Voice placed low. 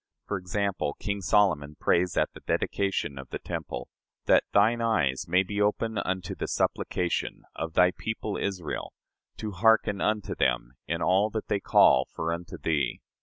Yes: very low, 95 Hz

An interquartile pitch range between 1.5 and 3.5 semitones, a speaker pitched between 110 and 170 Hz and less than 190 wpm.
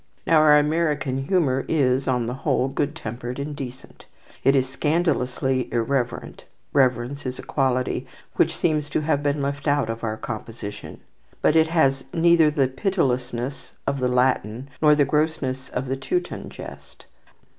Yes: average, 2.9 semitones; low, 135 Hz; average, 155 wpm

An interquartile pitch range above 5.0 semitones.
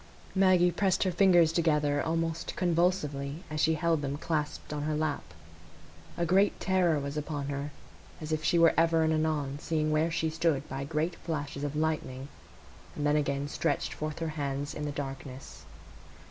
No: narrow, 2.4 semitones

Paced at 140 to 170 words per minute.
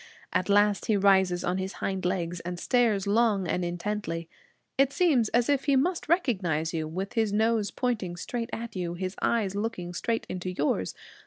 No: average, 180 wpm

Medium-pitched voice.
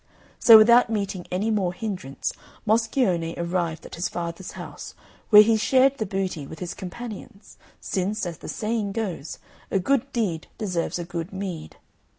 No: high, 195 Hz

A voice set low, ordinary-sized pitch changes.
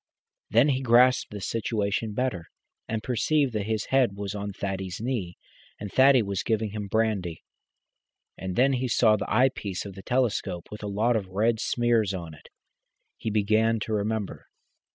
Yes: low, 110 Hz; average, 3.1 semitones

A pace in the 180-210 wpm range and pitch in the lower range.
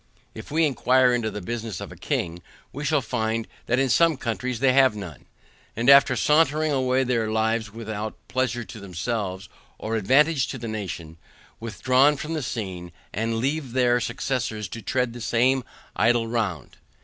No: average, 170 wpm; low, 120 Hz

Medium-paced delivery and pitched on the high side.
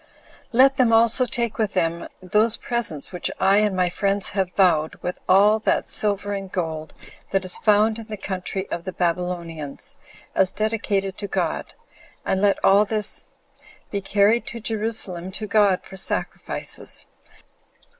Yes: average, 155 wpm; high, 200 Hz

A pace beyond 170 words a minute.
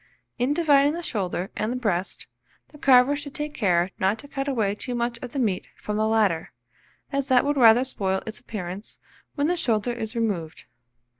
Yes: average, 190 wpm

